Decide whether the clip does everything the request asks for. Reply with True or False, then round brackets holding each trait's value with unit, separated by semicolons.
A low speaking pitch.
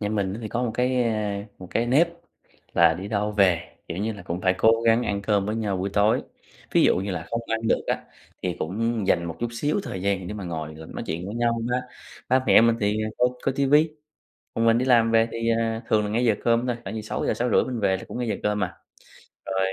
True (110 Hz)